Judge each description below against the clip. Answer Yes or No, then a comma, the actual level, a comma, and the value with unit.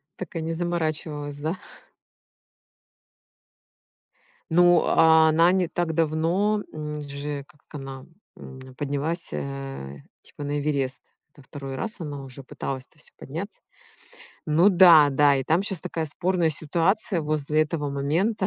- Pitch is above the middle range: No, medium, 155 Hz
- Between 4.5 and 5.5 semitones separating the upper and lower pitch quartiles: No, average, 3.2 semitones